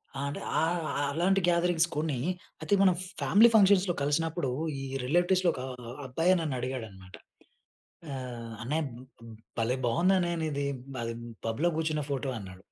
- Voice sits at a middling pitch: Yes, medium, 155 Hz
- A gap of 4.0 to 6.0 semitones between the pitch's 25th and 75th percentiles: Yes, wide, 5.5 semitones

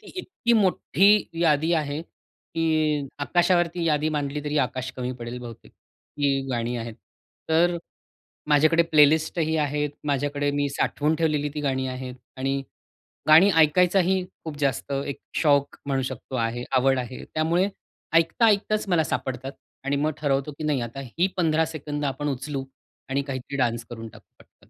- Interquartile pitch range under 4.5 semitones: Yes, average, 3.3 semitones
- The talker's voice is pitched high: No, medium, 145 Hz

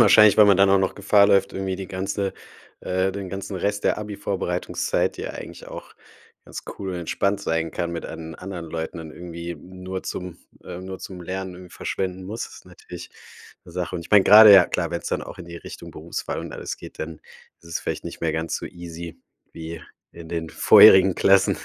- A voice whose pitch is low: Yes, very low, 95 Hz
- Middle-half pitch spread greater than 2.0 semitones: Yes, narrow, 2.5 semitones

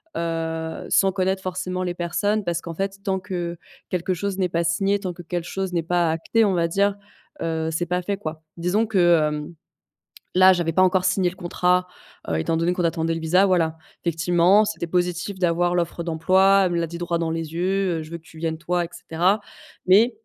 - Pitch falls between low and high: Yes, medium, 175 Hz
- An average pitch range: No, narrow, 2.2 semitones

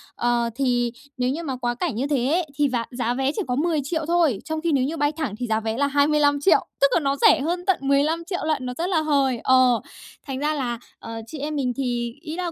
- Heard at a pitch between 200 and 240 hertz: No, very high, 280 Hz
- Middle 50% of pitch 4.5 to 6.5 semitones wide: No, average, 3.9 semitones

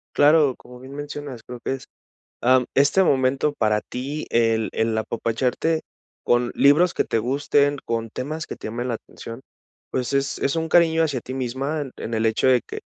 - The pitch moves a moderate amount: Yes, average, 3.6 semitones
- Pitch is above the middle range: No, low, 130 Hz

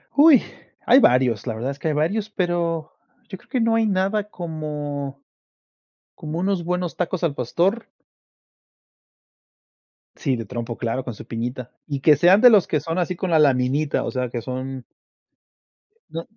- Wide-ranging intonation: Yes, wide, 6.0 semitones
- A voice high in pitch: No, medium, 155 Hz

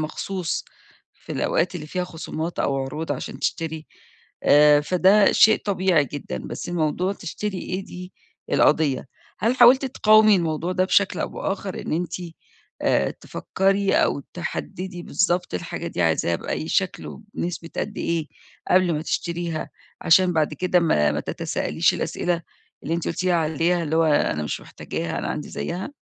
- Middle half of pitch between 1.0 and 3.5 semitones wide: Yes, average, 3.1 semitones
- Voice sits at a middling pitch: Yes, medium, 175 Hz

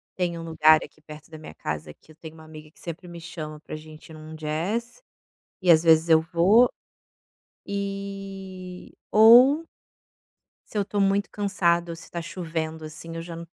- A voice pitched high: No, medium, 170 Hz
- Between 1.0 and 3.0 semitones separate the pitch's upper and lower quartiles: No, average, 3.7 semitones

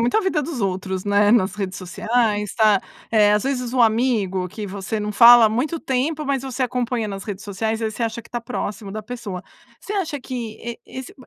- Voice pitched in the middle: No, high, 225 Hz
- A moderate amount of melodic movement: Yes, average, 3.4 semitones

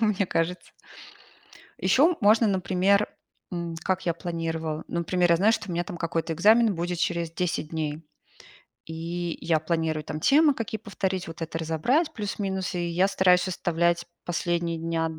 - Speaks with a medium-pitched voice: Yes, medium, 175 Hz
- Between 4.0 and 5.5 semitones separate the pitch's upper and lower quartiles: No, average, 2.8 semitones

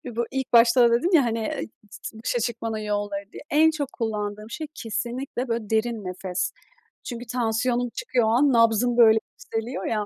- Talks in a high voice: Yes, high, 230 Hz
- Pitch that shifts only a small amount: Yes, narrow, 2.1 semitones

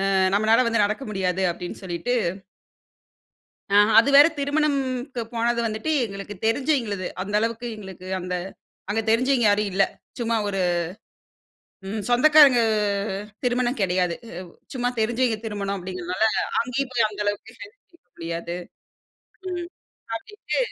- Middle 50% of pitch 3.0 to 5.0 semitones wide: Yes, average, 4.3 semitones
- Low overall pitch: No, high, 225 Hz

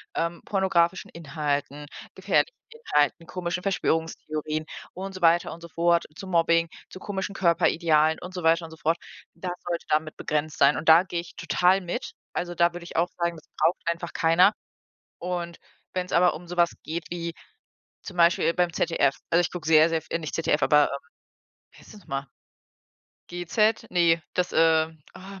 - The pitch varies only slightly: Yes, narrow, 1.8 semitones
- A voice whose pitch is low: No, medium, 170 Hz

